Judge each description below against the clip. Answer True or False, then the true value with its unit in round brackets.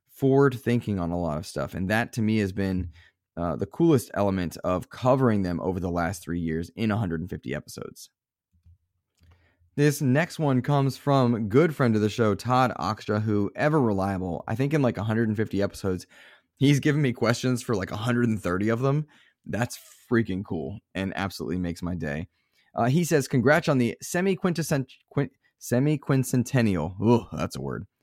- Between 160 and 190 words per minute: True (170 wpm)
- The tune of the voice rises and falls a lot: True (6.3 semitones)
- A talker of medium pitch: False (110 Hz)